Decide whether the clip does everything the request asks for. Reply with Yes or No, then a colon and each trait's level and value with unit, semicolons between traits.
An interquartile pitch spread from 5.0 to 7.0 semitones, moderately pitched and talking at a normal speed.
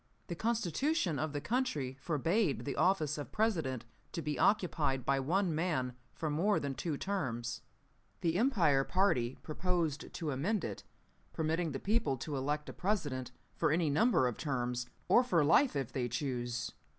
Yes: wide, 5.6 semitones; medium, 155 Hz; average, 160 wpm